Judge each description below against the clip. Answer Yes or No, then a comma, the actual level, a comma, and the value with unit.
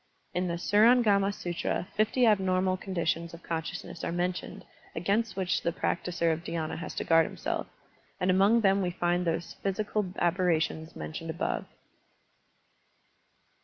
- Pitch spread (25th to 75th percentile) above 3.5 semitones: No, average, 2.7 semitones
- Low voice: No, medium, 180 Hz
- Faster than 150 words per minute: No, slow, 135 wpm